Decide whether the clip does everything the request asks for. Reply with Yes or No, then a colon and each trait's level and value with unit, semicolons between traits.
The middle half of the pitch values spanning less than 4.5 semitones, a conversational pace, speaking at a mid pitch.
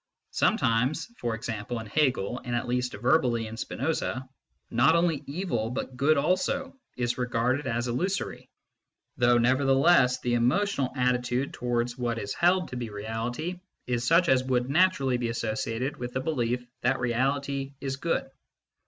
No: average, 2.8 semitones; average, 150 wpm; low, 125 Hz